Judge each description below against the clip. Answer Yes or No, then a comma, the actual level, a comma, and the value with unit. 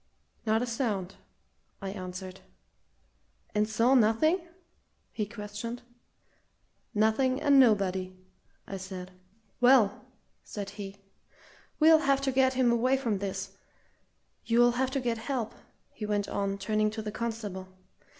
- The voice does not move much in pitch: No, average, 4.0 semitones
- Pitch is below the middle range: No, high, 220 Hz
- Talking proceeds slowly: Yes, slow, 125 wpm